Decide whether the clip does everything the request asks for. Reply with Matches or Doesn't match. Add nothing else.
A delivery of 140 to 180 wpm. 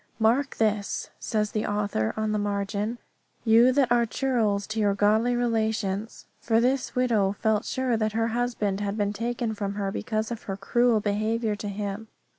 Matches